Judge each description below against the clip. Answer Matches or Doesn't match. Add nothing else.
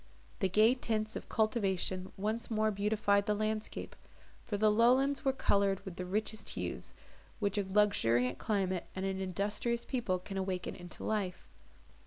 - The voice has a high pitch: Matches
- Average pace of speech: Matches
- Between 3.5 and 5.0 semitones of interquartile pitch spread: Doesn't match